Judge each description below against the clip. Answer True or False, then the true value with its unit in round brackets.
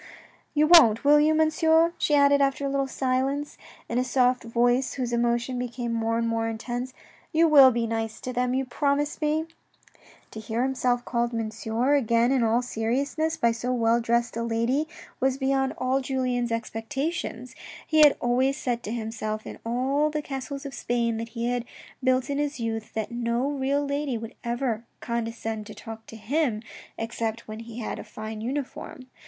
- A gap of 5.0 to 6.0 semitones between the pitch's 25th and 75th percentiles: False (3.2 semitones)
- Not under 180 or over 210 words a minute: True (185 wpm)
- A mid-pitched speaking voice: False (245 Hz)